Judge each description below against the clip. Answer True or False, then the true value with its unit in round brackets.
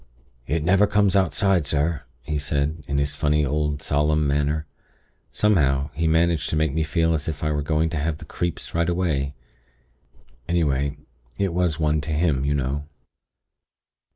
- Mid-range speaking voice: False (75 Hz)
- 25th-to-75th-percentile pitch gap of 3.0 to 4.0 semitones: False (2.5 semitones)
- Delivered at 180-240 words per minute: False (165 wpm)